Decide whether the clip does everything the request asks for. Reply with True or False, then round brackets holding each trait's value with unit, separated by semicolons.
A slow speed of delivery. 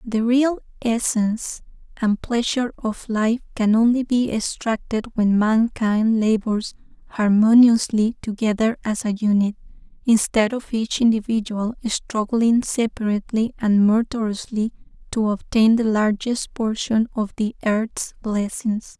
True (115 wpm)